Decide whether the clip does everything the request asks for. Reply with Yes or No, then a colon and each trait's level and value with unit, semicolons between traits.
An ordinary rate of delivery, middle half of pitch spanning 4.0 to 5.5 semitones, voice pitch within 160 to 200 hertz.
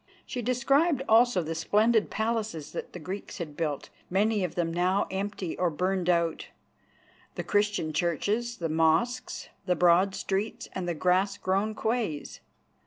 Yes: average, 150 wpm; average, 4.3 semitones; high, 190 Hz